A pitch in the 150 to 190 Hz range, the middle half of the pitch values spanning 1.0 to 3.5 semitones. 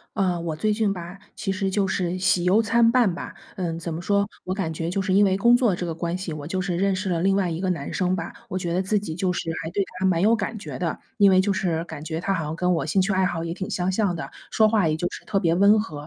Yes: medium, 185 Hz; average, 2.7 semitones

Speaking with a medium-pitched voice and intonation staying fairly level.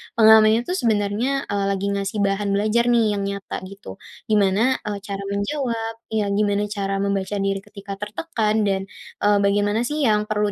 No: high, 205 Hz; narrow, 1.8 semitones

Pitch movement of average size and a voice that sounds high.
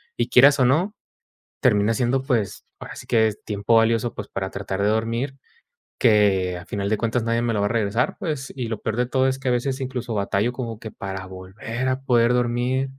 No: average, 3.5 semitones; low, 115 Hz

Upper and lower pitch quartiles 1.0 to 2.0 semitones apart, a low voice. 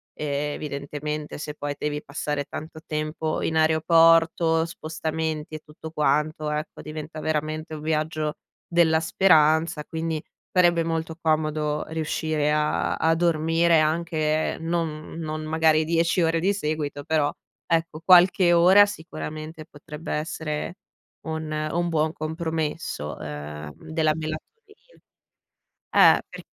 No: narrow, 1.3 semitones; medium, 155 Hz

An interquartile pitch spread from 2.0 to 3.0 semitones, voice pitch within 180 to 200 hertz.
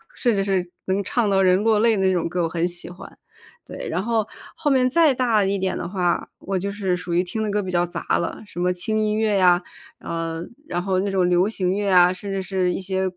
Yes: average, 2.7 semitones; high, 190 Hz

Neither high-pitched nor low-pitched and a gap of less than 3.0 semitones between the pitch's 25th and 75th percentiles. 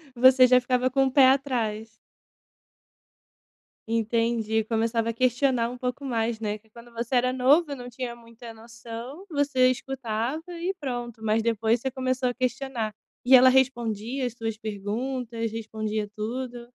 No: high, 240 Hz; narrow, 2.4 semitones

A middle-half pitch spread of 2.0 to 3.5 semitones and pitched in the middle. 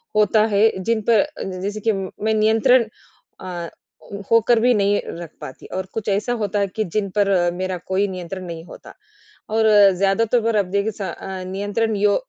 No: average, 2.7 semitones; high, 205 Hz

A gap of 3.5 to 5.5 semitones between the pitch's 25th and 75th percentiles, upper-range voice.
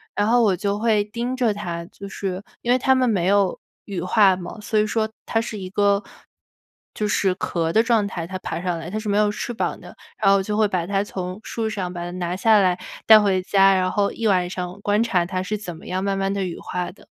No: average, 2.7 semitones; high, 200 Hz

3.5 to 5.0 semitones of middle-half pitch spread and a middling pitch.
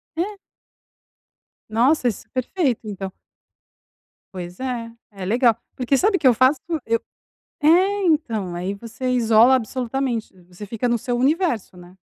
No: average, 4.1 semitones; high, 240 Hz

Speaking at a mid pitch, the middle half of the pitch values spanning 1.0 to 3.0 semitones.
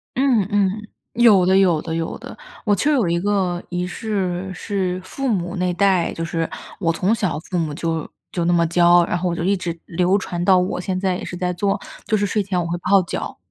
Yes: medium, 180 Hz; narrow, 2.5 semitones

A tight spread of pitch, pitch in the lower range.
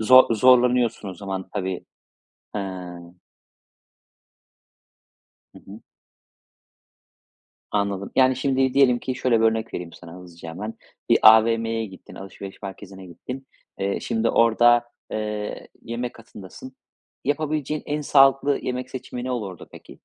No: average, 4.6 semitones; low, 115 Hz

